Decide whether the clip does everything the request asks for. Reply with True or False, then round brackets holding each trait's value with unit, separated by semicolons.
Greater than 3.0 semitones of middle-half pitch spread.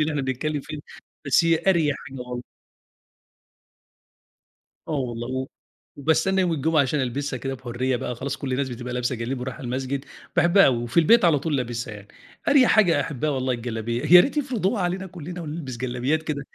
True (4.7 semitones)